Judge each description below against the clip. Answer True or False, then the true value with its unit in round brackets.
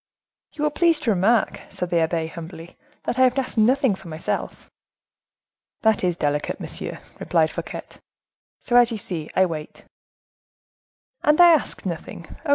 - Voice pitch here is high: True (195 Hz)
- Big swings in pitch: True (7.5 semitones)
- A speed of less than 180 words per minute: True (160 wpm)